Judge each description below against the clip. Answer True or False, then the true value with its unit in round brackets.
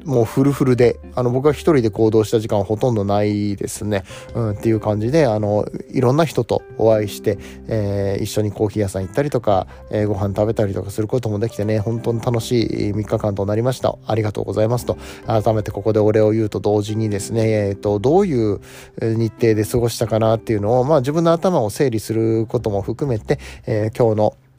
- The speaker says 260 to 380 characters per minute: False (430 characters per minute)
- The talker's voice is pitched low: True (110 Hz)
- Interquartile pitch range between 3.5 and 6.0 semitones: False (2.5 semitones)